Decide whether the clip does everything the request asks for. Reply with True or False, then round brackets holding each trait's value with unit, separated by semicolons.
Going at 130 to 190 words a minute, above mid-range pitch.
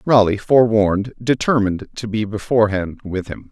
False (135 wpm; 110 Hz)